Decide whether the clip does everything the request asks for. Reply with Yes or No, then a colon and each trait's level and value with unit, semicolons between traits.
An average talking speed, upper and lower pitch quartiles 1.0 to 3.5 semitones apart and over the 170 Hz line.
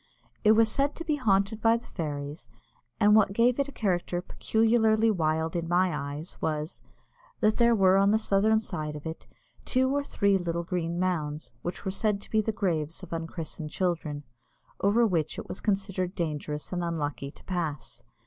No: average, 185 wpm; average, 5.2 semitones; medium, 185 Hz